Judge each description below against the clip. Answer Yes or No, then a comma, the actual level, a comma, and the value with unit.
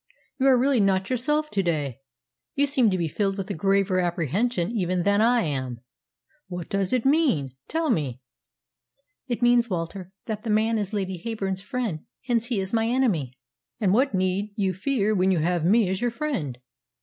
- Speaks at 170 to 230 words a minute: Yes, average, 185 wpm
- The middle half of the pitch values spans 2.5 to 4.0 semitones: No, average, 5.1 semitones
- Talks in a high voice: Yes, high, 200 Hz